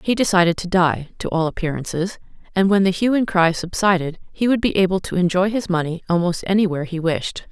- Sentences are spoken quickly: Yes, fast, 210 wpm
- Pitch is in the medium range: Yes, medium, 180 Hz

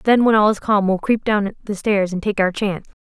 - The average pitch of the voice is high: Yes, high, 205 Hz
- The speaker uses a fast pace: Yes, fast, 275 wpm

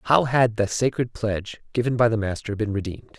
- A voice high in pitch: No, low, 115 Hz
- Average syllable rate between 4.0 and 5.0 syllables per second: No, 6.1 syllables/s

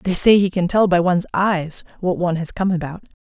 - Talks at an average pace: No, fast, 240 wpm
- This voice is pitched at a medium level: Yes, medium, 180 Hz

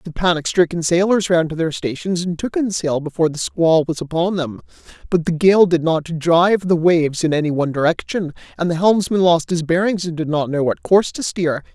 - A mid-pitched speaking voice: Yes, medium, 170 Hz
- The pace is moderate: No, fast, 225 wpm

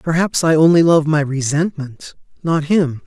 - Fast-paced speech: No, average, 155 wpm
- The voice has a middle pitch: Yes, medium, 155 Hz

